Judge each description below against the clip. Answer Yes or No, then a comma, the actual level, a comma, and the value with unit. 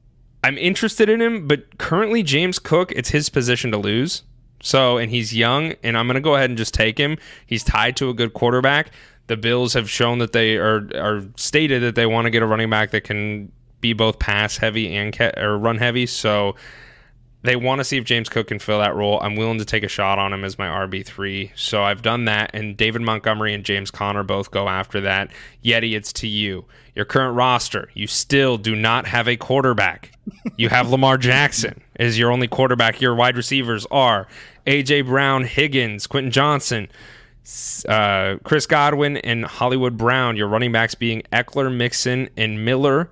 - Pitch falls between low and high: No, low, 120 Hz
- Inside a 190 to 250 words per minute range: Yes, average, 200 wpm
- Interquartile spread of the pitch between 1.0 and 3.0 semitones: No, average, 3.4 semitones